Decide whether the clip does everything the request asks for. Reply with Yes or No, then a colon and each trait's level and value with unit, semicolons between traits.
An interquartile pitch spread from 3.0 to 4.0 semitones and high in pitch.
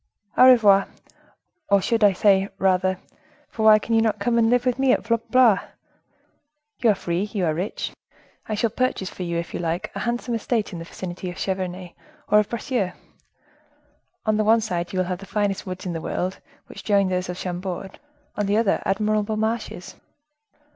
Yes: average, 3.3 semitones; high, 200 Hz